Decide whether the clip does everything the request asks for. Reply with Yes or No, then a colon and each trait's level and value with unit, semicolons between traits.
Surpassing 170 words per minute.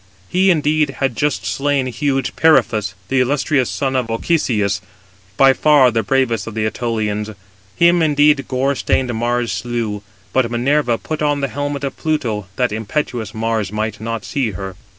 No: average, 160 wpm